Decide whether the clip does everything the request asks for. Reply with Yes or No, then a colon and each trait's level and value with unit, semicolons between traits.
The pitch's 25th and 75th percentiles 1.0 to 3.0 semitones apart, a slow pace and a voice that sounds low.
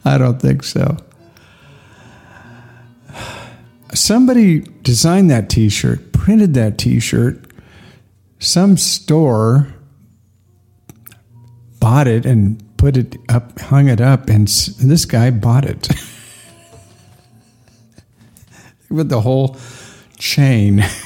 No: average, 4.0 semitones; slow, 95 wpm; low, 120 Hz